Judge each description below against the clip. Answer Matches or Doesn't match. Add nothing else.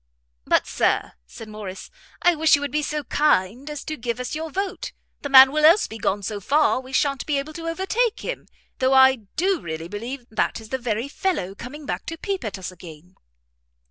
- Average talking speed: Doesn't match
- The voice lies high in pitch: Matches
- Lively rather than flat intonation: Matches